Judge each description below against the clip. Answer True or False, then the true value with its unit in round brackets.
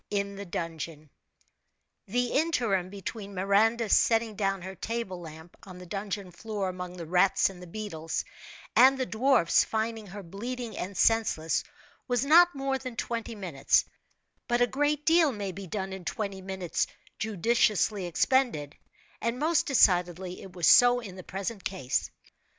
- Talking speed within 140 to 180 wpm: True (150 wpm)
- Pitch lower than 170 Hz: False (200 Hz)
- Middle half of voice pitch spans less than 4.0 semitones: False (4.5 semitones)